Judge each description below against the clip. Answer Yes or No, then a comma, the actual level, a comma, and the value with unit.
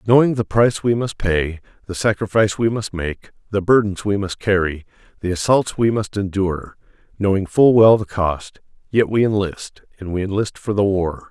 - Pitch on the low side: Yes, low, 100 Hz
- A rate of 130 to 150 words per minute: No, average, 175 wpm